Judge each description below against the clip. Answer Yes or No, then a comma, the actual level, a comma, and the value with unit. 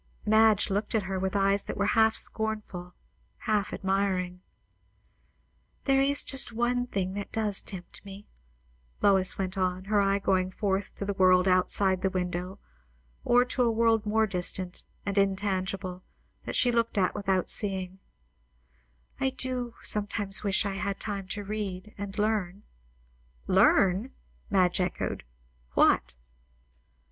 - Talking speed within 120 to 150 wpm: Yes, average, 140 wpm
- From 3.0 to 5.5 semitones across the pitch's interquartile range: No, narrow, 2.4 semitones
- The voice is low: No, high, 200 Hz